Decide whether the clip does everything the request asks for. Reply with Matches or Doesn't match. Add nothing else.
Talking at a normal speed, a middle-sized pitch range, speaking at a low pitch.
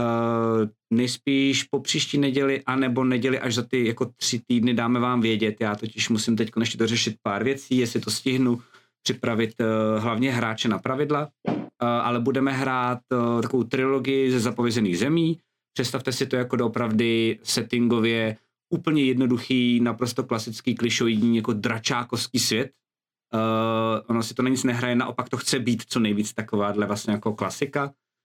Doesn't match